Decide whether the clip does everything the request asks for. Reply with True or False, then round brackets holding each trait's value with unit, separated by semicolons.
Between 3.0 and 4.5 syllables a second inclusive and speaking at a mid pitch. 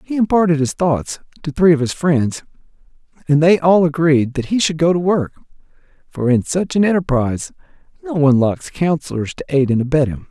False (5.4 syllables/s; 155 Hz)